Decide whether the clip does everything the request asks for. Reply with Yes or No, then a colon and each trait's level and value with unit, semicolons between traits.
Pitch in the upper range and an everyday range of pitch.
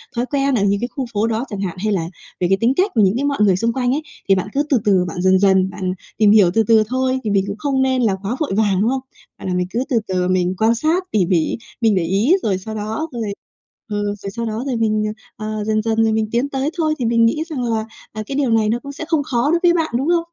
Yes: high, 220 Hz; average, 4.7 semitones